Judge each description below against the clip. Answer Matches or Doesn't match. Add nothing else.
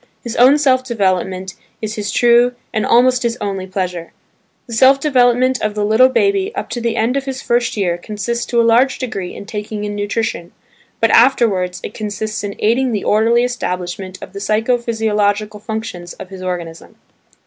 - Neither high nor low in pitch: Doesn't match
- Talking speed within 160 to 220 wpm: Matches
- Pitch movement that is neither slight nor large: Matches